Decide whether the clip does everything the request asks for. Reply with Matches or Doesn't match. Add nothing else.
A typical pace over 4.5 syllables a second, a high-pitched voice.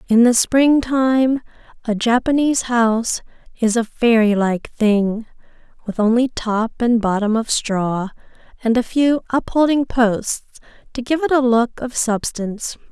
Doesn't match